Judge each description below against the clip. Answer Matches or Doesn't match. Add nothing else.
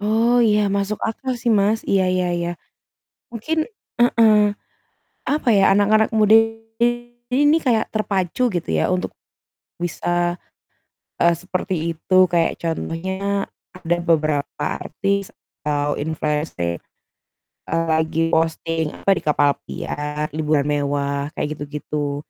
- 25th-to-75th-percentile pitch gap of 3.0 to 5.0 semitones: Doesn't match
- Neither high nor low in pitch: Matches